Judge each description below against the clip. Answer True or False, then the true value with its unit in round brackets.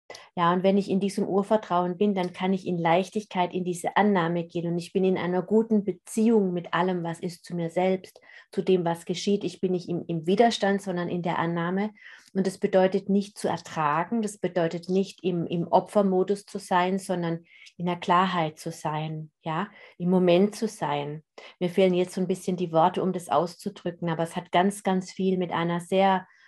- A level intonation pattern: True (2.2 semitones)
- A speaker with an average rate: False (205 wpm)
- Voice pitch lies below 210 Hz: True (185 Hz)